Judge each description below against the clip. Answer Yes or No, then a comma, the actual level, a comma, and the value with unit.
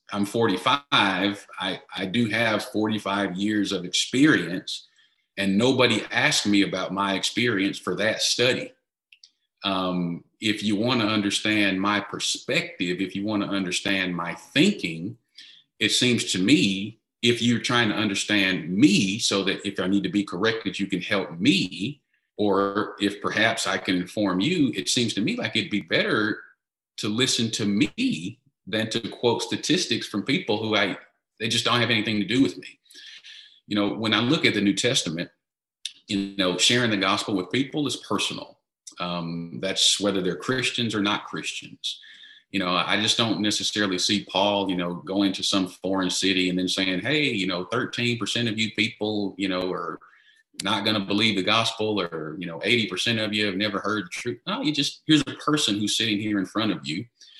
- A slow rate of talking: No, average, 185 wpm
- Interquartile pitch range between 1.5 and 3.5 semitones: Yes, average, 2.7 semitones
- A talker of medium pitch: No, low, 105 Hz